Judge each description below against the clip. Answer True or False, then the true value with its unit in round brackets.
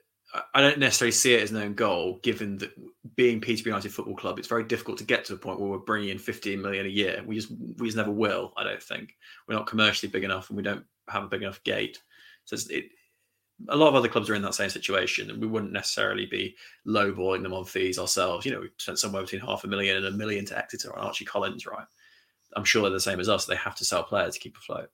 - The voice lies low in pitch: True (105 Hz)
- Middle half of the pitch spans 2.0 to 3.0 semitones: True (2.6 semitones)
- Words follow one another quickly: True (265 wpm)